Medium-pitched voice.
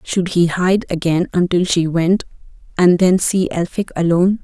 Yes: medium, 180 Hz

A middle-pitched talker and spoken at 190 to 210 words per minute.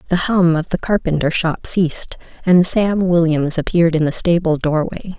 No: medium, 170 Hz; average, 175 wpm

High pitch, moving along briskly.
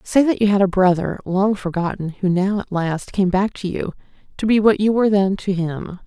Yes: high, 195 Hz; fast, 235 wpm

